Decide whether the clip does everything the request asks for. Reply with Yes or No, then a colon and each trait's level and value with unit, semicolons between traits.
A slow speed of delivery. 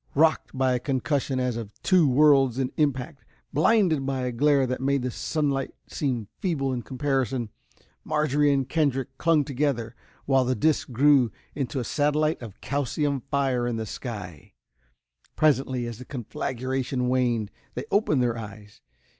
No: average, 155 wpm